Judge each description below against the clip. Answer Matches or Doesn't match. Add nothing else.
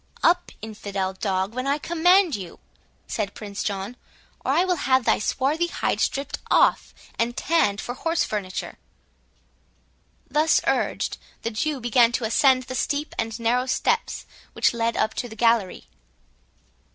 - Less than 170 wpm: Matches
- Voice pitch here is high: Matches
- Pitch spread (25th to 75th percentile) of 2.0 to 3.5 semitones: Doesn't match